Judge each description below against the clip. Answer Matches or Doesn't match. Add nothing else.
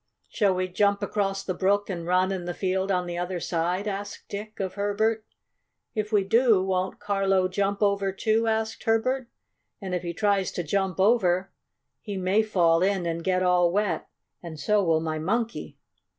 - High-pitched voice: Matches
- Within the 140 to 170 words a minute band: Doesn't match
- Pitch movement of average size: Doesn't match